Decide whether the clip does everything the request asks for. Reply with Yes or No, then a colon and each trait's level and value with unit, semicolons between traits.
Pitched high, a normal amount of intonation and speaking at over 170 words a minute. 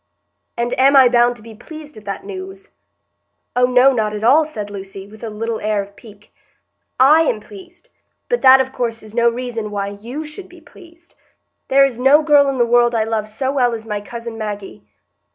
Yes: high, 235 Hz; average, 4.3 semitones; fast, 205 wpm